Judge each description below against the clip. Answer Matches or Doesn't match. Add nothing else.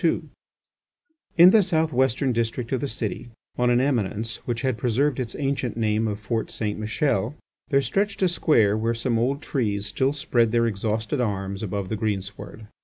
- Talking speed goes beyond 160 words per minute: Matches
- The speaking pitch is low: Matches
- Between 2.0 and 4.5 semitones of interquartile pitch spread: Matches